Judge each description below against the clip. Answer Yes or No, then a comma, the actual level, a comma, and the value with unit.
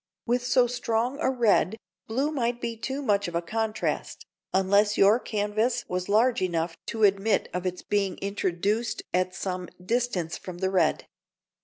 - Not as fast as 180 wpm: Yes, average, 160 wpm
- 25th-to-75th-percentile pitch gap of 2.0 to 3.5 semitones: No, average, 4.4 semitones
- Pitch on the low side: No, high, 210 Hz